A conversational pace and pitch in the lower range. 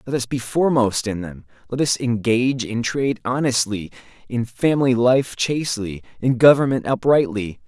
Yes: average, 150 wpm; low, 120 Hz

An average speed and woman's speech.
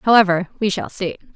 Yes: average, 180 wpm; female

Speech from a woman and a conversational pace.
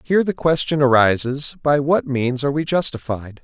No: male; average, 175 wpm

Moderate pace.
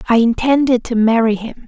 Yes: average, 180 wpm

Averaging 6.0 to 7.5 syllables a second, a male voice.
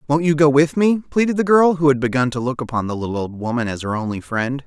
Yes: 6.3 syllables/s; male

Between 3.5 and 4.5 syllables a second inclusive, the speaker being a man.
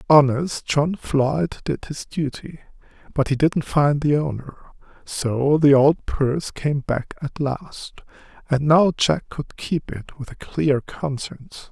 Yes: 3.7 syllables/s; male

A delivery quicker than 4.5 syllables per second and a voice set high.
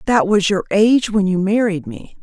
Yes: 5.1 syllables/s; high, 200 Hz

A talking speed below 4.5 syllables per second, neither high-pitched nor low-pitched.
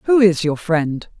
Yes: 3.6 syllables/s; medium, 180 Hz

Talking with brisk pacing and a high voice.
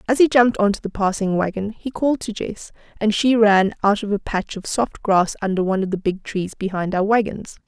Yes: fast, 240 wpm; high, 205 Hz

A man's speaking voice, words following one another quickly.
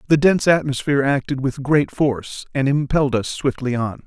No: male; average, 175 wpm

